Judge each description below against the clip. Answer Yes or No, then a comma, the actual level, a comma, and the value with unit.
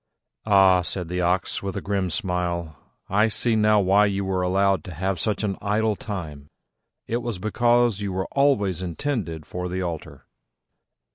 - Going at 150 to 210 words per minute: Yes, average, 165 wpm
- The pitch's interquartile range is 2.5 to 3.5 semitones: Yes, average, 2.8 semitones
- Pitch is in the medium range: No, very low, 95 Hz